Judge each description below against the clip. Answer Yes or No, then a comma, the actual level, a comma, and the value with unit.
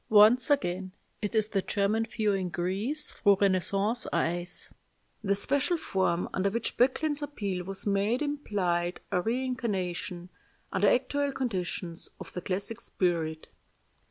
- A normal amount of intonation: Yes, average, 4.7 semitones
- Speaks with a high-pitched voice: Yes, high, 200 Hz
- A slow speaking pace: Yes, slow, 130 wpm